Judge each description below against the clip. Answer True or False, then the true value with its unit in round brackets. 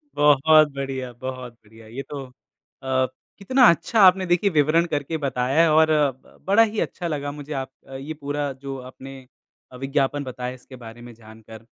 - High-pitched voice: False (140 Hz)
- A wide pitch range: False (3.4 semitones)